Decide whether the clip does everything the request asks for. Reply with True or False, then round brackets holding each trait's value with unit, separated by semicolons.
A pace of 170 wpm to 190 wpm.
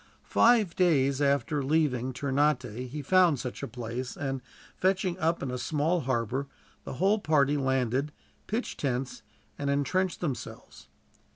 False (135 wpm)